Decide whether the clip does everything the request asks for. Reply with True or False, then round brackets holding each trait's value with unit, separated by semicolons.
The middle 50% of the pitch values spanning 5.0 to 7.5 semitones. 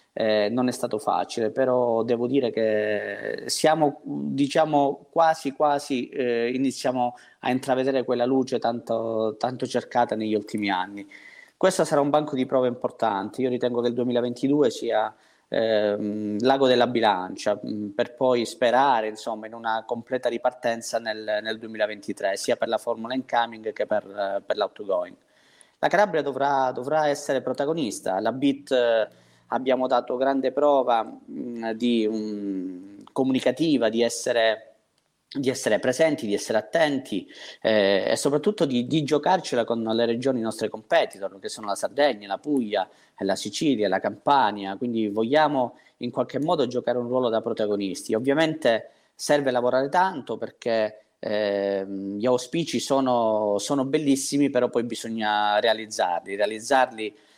False (3.5 semitones)